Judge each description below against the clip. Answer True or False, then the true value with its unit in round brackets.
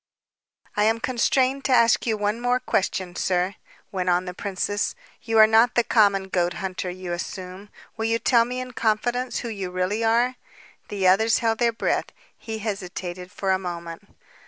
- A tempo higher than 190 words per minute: False (175 wpm)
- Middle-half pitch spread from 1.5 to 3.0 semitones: False (3.8 semitones)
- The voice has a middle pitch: False (210 Hz)